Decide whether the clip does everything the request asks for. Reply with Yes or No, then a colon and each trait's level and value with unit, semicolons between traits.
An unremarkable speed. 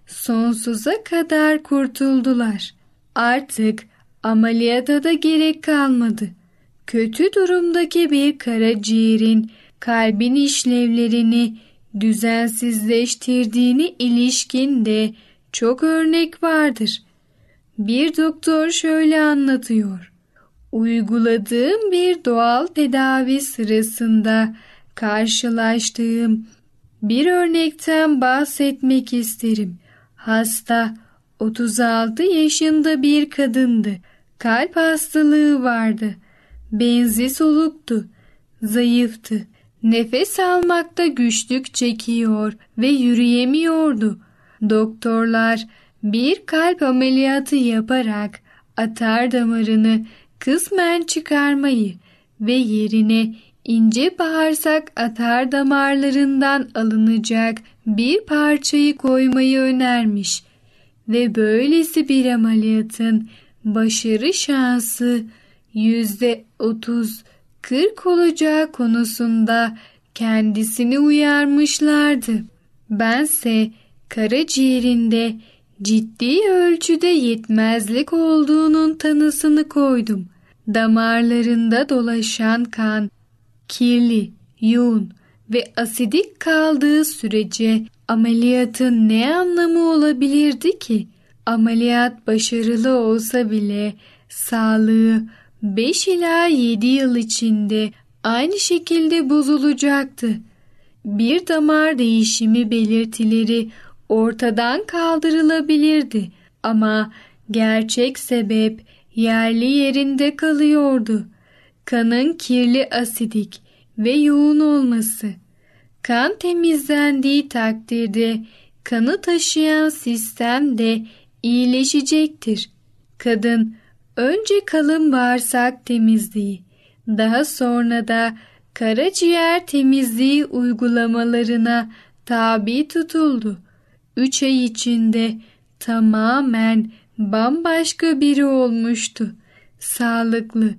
No: slow, 70 wpm